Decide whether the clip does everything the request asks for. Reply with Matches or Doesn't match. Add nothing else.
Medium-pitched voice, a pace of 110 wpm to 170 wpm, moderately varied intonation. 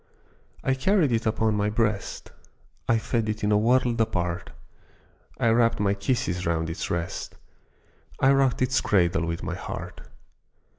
Doesn't match